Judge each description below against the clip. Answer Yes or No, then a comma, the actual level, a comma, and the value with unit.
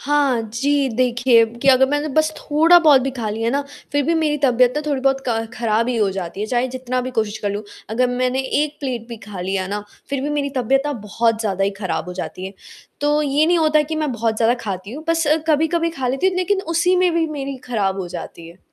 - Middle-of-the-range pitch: No, very high, 255 Hz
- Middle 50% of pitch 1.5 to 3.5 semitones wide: No, average, 5.1 semitones